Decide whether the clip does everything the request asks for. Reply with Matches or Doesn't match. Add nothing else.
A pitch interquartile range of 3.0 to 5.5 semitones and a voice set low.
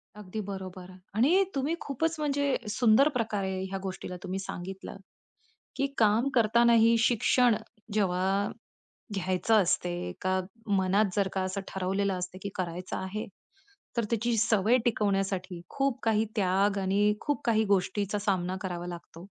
Doesn't match